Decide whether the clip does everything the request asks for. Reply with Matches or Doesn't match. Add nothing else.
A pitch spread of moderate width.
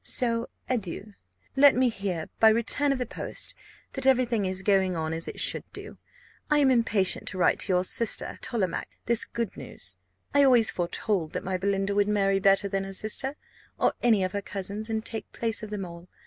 Matches